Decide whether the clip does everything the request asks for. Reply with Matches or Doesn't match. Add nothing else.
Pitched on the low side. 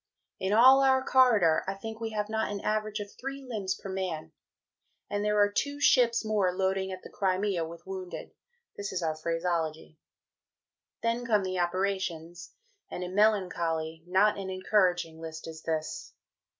Doesn't match